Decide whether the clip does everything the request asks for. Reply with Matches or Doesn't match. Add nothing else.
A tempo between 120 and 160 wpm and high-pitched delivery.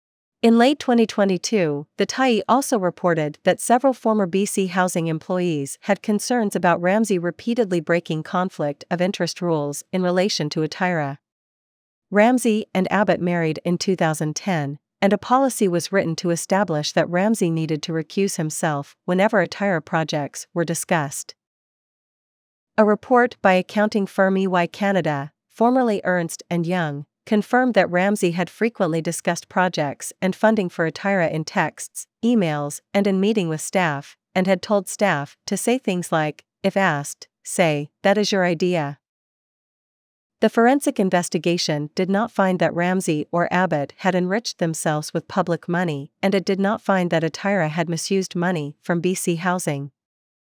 Doesn't match